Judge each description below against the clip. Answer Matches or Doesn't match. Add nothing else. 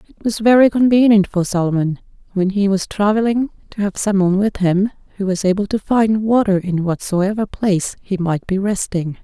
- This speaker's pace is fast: Doesn't match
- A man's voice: Doesn't match